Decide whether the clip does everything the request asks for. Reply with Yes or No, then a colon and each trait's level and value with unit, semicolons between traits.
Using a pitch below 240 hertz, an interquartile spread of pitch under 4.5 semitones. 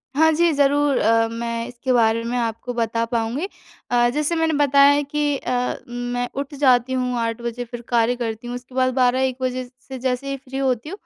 No: very high, 250 Hz; narrow, 2.5 semitones